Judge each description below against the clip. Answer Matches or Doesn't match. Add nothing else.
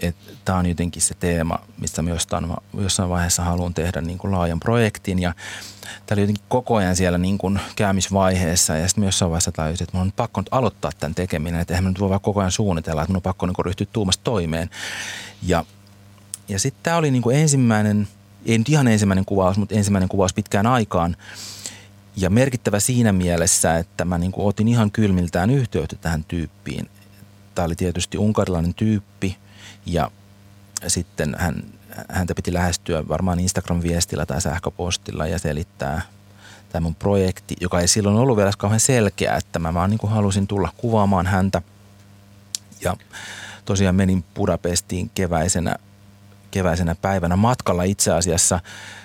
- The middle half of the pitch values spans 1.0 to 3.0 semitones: Matches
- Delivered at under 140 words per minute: Doesn't match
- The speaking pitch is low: Matches